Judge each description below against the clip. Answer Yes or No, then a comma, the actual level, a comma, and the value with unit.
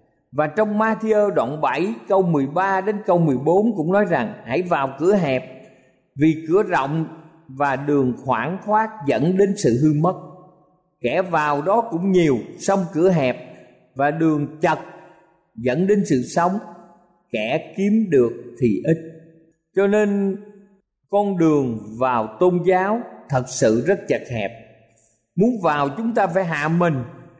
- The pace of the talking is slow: Yes, slow, 150 wpm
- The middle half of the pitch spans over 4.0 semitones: Yes, wide, 5.6 semitones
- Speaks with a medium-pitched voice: Yes, medium, 170 Hz